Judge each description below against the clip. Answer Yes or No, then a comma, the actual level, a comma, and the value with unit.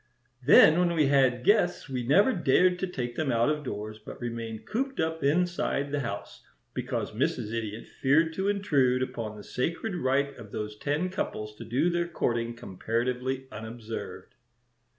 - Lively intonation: Yes, wide, 6.2 semitones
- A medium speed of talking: Yes, average, 165 wpm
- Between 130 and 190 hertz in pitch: Yes, low, 135 Hz